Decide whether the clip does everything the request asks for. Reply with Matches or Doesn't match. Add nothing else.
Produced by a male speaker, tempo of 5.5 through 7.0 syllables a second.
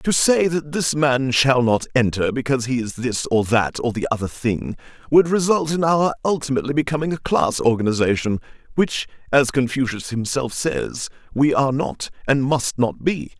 Doesn't match